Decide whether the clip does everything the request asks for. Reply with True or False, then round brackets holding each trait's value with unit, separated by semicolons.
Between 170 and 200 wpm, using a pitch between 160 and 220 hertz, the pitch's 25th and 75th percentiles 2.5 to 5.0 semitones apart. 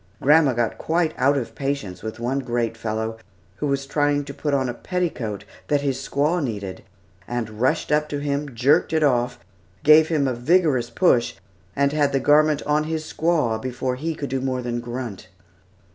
False (185 wpm; 135 Hz; 3.8 semitones)